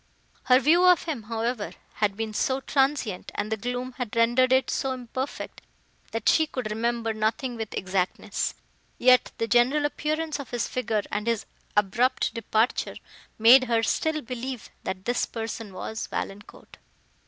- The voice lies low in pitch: No, high, 240 Hz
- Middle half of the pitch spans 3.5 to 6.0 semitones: No, average, 2.9 semitones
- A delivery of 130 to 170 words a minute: Yes, average, 155 wpm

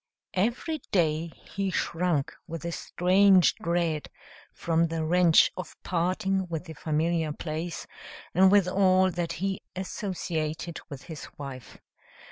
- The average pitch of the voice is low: No, medium, 170 Hz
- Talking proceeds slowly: Yes, slow, 125 wpm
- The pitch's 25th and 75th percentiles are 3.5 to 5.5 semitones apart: No, average, 2.7 semitones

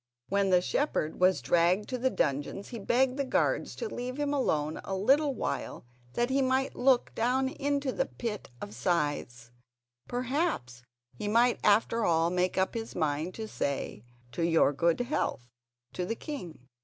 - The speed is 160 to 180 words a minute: Yes, average, 170 wpm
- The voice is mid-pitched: No, high, 210 Hz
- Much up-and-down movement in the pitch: Yes, wide, 7.6 semitones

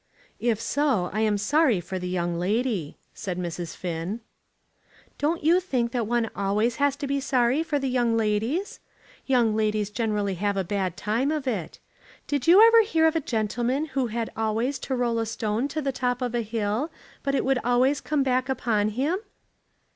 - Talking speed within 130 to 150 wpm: No, average, 190 wpm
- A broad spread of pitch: No, average, 4.7 semitones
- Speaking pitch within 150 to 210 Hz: No, high, 235 Hz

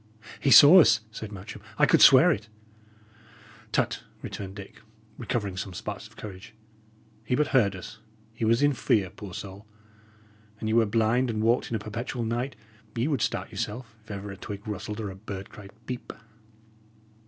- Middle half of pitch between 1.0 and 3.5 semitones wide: Yes, average, 2.8 semitones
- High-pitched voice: No, low, 110 Hz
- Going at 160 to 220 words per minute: Yes, average, 175 wpm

